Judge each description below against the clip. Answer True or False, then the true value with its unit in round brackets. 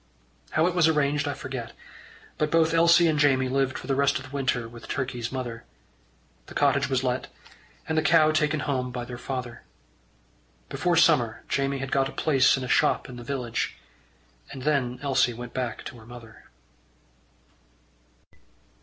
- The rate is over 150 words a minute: True (170 wpm)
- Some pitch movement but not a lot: True (3.5 semitones)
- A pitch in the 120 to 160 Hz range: True (135 Hz)